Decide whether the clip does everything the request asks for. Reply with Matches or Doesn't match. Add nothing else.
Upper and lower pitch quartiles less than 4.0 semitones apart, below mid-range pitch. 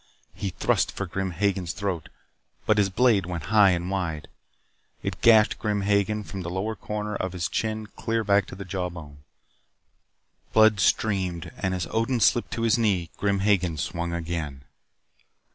Matches